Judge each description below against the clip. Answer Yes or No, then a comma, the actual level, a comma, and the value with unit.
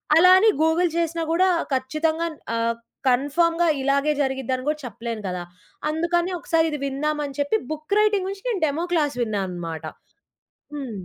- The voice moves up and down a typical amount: Yes, average, 4.4 semitones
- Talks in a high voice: Yes, very high, 300 Hz